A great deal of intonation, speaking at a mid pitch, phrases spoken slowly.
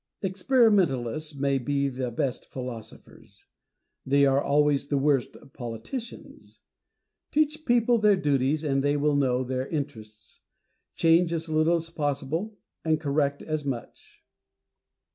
No: average, 3.7 semitones; medium, 145 Hz; slow, 125 wpm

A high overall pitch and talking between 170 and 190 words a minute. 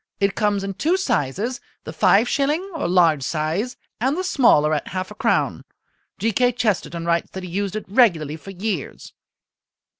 Yes: high, 200 Hz; average, 175 wpm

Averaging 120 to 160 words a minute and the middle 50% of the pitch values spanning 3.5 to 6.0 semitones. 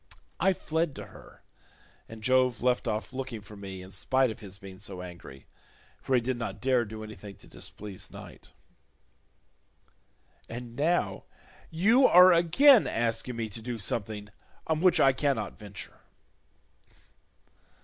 Yes: average, 145 wpm; average, 4.7 semitones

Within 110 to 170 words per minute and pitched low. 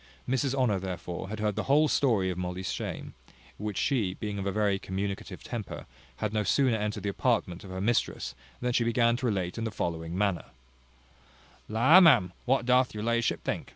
No: average, 190 wpm; low, 105 Hz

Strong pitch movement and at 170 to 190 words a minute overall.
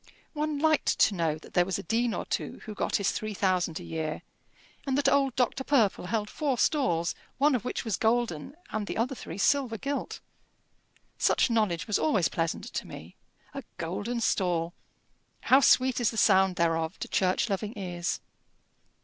Yes: wide, 6.3 semitones; average, 180 wpm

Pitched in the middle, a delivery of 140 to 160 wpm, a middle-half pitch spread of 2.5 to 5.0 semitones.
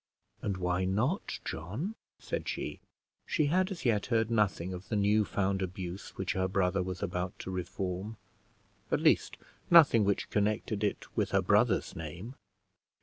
No: low, 100 Hz; average, 155 wpm; average, 3.3 semitones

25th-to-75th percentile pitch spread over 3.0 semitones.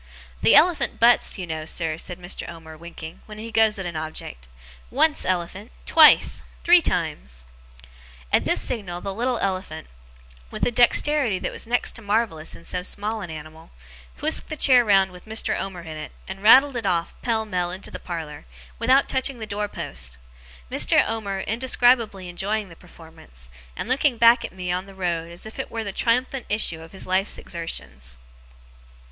Yes: average, 5.3 semitones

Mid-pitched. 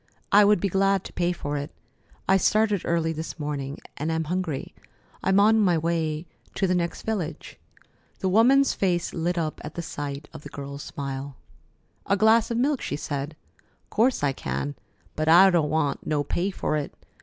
Yes: medium, 170 Hz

